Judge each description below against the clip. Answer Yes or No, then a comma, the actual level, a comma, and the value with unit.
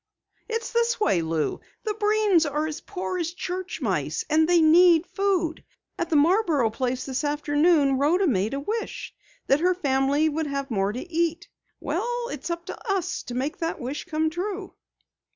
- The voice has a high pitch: Yes, very high, 320 Hz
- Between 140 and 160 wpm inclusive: No, average, 175 wpm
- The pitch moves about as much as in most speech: Yes, average, 4.7 semitones